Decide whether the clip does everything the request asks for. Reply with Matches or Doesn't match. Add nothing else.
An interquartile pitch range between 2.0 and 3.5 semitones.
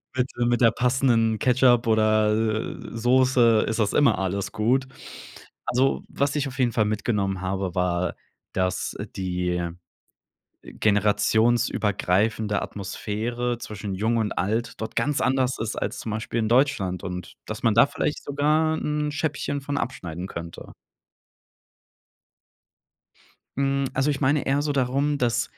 Doesn't match